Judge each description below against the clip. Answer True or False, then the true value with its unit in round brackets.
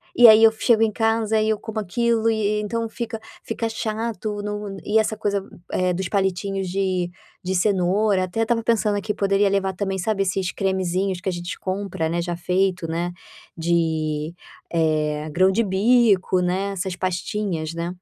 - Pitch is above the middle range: True (195 Hz)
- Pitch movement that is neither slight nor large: True (3.3 semitones)